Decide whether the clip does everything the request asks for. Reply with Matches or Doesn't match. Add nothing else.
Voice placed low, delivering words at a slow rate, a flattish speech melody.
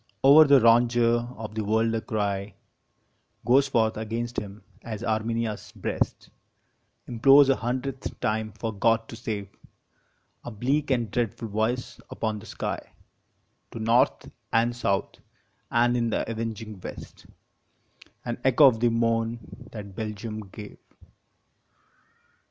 Matches